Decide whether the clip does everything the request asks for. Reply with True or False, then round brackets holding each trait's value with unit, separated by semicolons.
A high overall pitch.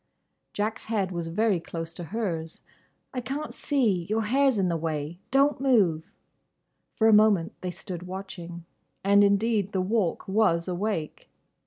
True (195 Hz)